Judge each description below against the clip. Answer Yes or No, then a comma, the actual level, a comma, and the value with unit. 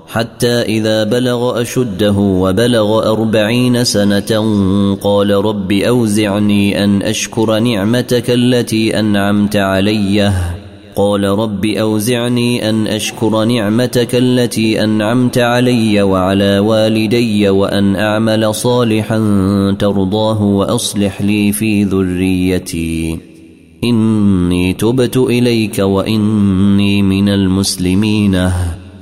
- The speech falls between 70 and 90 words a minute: Yes, average, 85 wpm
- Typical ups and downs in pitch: No, narrow, 2.1 semitones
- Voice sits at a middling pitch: No, low, 105 Hz